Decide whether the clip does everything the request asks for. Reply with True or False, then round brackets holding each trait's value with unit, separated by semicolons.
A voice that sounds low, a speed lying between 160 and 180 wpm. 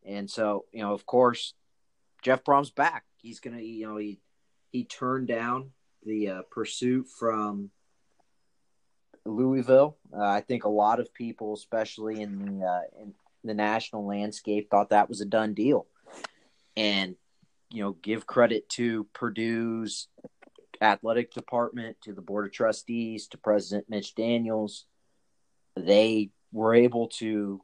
False (110 Hz; 145 wpm)